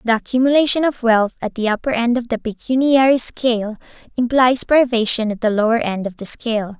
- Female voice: Yes, female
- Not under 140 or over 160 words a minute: No, average, 185 wpm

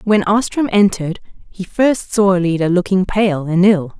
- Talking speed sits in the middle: Yes, average, 165 wpm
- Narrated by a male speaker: No, female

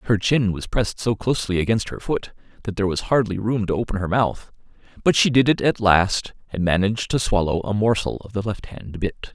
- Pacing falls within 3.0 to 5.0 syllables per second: No, 5.7 syllables/s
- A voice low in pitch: Yes, low, 105 Hz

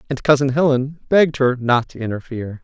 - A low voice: Yes, low, 130 Hz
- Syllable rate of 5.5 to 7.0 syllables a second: Yes, 6.0 syllables/s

